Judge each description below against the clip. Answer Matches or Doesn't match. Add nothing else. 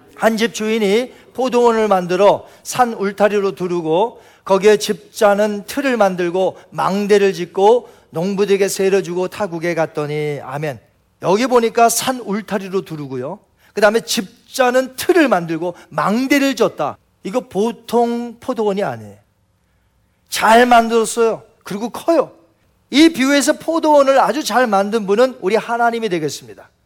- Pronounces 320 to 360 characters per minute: Doesn't match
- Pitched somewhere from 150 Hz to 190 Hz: Doesn't match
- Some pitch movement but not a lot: Matches